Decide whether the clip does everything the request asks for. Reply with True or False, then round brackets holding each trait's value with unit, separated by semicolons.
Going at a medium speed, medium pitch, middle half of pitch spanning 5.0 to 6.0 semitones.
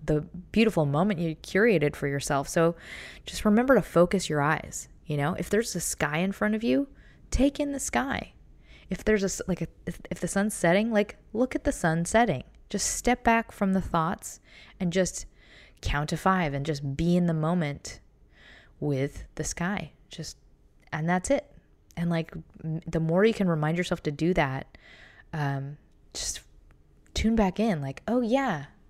True (180 wpm; 175 Hz; 5.4 semitones)